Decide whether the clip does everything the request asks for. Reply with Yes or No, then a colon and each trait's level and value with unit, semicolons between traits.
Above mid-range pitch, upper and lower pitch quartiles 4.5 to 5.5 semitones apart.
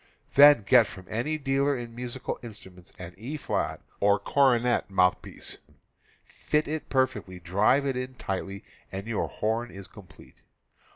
No: low, 120 Hz; average, 5.2 semitones